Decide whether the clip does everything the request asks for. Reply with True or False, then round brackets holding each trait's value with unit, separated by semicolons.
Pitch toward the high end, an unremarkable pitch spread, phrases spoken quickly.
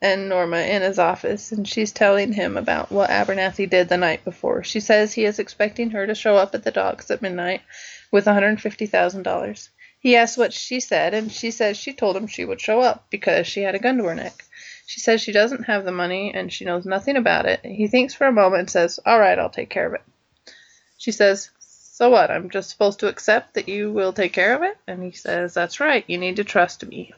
True (205 Hz; 3.3 semitones; 240 wpm)